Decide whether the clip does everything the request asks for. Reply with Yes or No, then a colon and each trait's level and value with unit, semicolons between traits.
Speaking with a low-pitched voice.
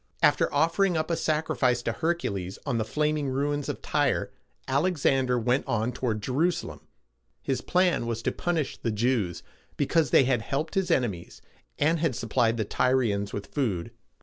Yes: low, 130 Hz